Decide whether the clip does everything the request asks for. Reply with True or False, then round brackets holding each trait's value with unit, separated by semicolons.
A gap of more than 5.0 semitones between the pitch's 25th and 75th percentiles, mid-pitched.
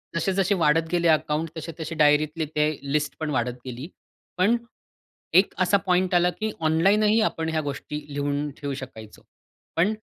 False (3.4 semitones; 160 Hz)